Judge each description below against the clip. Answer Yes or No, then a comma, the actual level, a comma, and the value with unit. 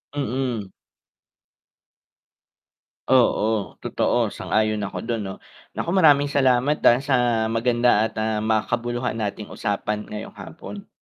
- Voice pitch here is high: No, low, 115 Hz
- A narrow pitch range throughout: No, average, 3.0 semitones